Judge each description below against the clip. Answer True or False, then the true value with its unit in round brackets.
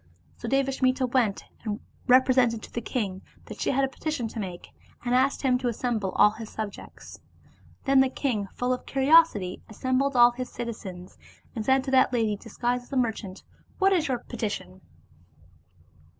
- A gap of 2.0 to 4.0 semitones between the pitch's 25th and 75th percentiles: True (3.3 semitones)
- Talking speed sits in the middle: True (175 wpm)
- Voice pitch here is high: True (245 Hz)